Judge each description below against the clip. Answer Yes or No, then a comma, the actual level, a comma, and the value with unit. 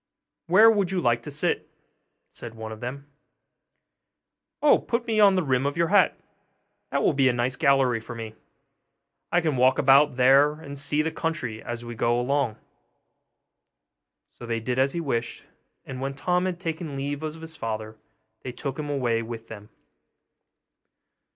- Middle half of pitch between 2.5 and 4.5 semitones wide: No, average, 5.1 semitones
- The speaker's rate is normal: Yes, average, 170 wpm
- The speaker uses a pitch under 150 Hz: Yes, low, 135 Hz